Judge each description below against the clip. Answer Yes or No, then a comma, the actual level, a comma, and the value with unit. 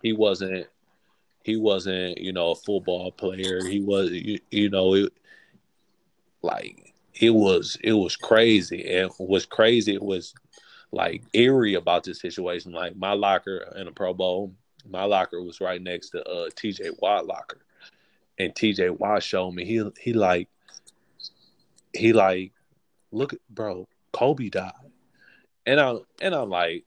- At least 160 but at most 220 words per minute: No, average, 150 wpm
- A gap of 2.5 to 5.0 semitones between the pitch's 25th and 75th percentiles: Yes, average, 3.3 semitones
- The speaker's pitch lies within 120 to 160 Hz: No, very low, 95 Hz